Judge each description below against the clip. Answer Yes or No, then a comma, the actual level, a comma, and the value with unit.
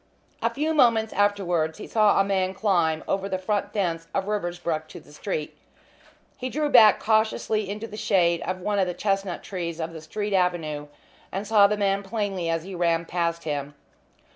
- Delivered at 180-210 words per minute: Yes, average, 190 wpm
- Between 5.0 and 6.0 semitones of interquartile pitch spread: No, average, 3.7 semitones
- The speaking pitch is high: Yes, high, 195 Hz